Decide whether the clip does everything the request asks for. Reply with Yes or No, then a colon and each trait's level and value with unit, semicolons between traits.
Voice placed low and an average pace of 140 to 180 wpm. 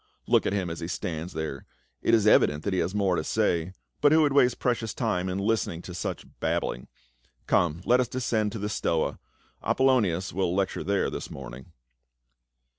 No: very low, 95 Hz; average, 190 wpm